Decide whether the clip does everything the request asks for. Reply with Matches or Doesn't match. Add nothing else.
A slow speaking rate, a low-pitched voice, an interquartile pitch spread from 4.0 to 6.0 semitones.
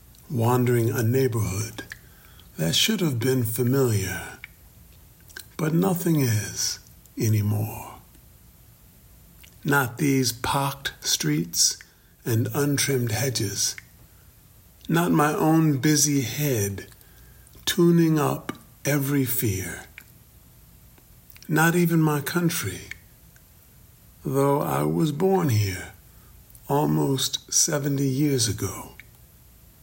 Matches